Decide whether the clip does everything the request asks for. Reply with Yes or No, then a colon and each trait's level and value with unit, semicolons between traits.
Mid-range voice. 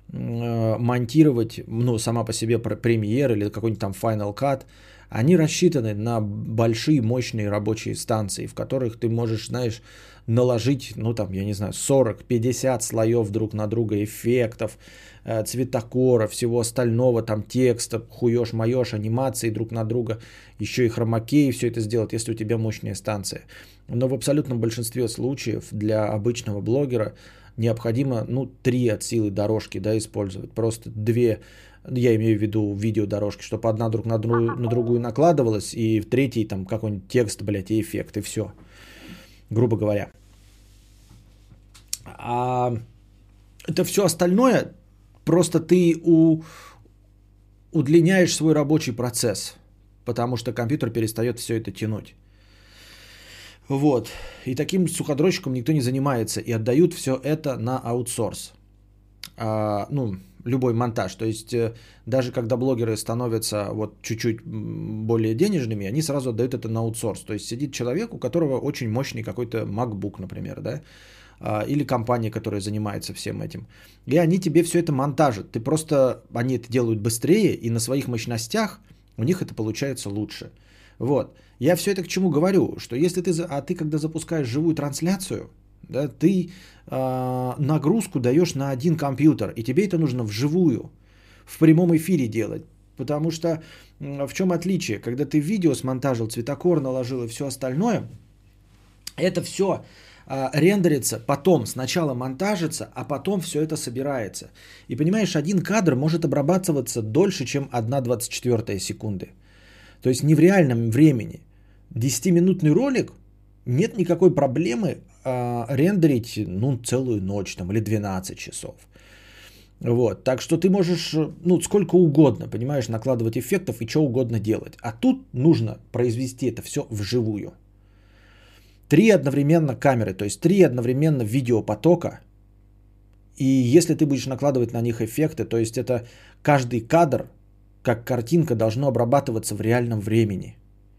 No: low, 120 Hz